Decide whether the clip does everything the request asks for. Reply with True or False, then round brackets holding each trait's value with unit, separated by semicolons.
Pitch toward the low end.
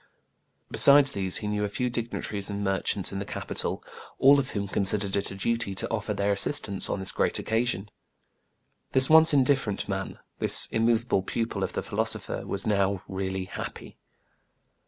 True (100 Hz)